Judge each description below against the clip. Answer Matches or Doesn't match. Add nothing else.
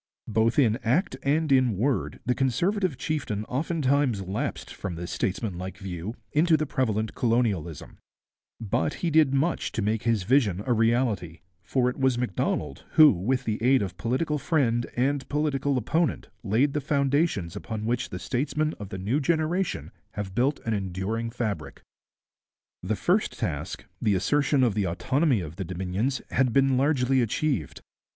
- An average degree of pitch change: Doesn't match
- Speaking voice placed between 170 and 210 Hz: Doesn't match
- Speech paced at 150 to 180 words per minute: Matches